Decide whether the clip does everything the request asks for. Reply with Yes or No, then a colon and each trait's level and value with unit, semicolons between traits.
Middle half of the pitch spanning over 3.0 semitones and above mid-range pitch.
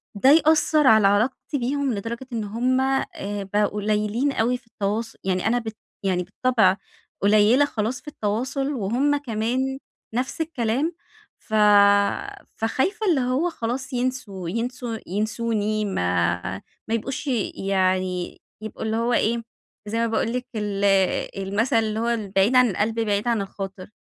Yes: average, 3.8 semitones; high, 225 Hz